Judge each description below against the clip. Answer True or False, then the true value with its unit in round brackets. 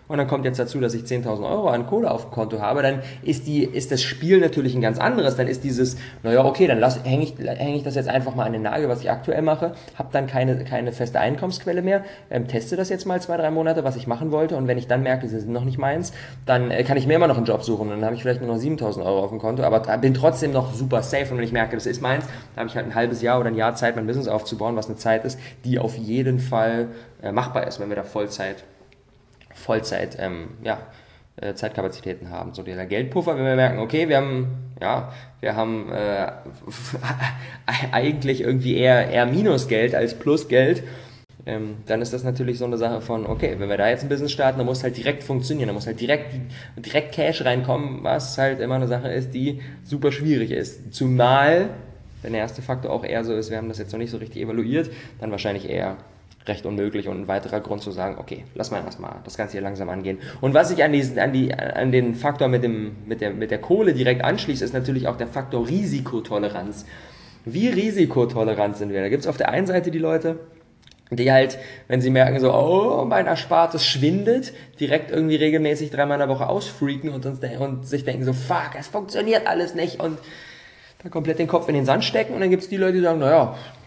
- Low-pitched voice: True (130 Hz)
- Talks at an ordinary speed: False (230 wpm)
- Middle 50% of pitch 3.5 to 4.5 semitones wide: True (4.0 semitones)